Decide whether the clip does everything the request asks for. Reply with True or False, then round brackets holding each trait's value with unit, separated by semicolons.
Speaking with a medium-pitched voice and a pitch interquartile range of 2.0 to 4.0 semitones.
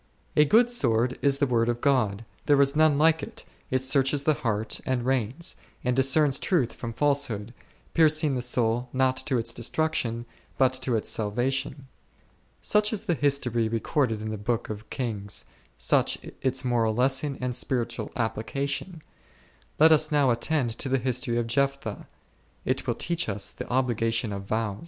False (130 Hz; 3.5 semitones)